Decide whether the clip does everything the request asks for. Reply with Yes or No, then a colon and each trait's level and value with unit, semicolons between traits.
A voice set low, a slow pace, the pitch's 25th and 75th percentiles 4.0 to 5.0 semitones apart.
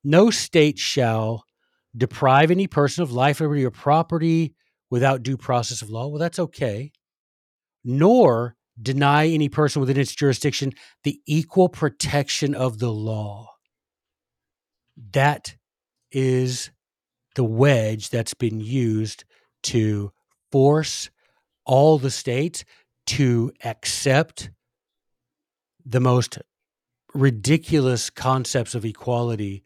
Yes: low, 130 Hz; slow, 105 wpm; average, 4.4 semitones